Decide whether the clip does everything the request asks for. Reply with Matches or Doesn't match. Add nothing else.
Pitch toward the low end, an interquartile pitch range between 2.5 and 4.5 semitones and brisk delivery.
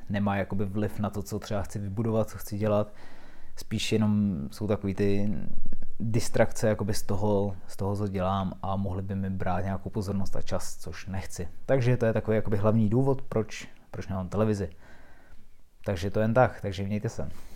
Doesn't match